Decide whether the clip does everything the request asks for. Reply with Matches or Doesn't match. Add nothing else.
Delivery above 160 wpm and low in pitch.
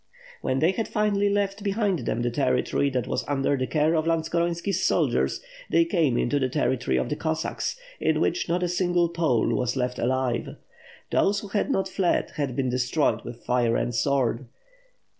Doesn't match